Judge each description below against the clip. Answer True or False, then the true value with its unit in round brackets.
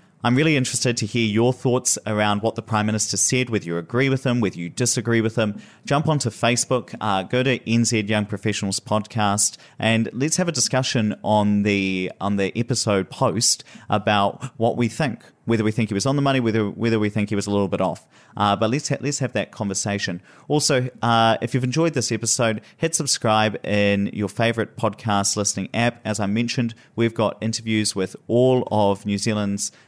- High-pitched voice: False (110 Hz)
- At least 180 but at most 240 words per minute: True (200 wpm)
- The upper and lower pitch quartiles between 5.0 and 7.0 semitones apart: False (3.3 semitones)